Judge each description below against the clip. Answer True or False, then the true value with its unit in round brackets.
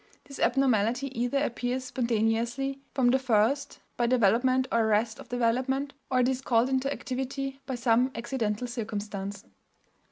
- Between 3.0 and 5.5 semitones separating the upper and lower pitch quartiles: False (2.6 semitones)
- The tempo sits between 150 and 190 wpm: False (140 wpm)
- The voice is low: False (245 Hz)